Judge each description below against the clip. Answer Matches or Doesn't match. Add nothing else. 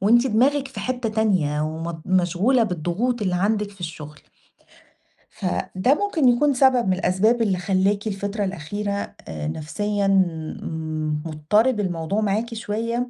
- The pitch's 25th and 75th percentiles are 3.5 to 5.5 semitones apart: Matches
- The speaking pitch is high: Matches